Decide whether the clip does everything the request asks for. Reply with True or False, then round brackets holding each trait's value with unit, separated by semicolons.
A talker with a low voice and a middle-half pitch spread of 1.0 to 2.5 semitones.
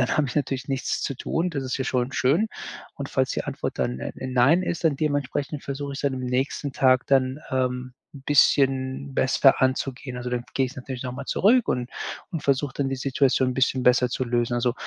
True (130 Hz; 1.7 semitones)